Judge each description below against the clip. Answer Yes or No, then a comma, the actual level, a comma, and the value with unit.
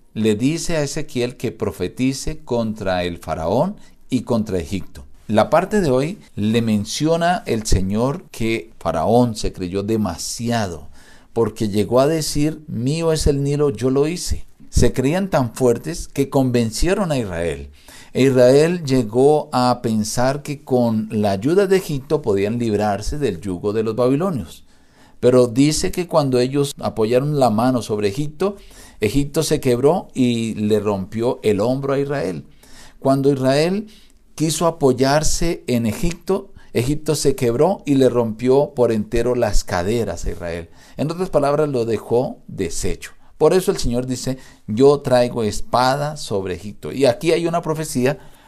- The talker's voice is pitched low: Yes, low, 125 Hz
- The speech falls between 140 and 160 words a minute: Yes, average, 150 wpm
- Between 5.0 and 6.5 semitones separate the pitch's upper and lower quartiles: Yes, average, 5.3 semitones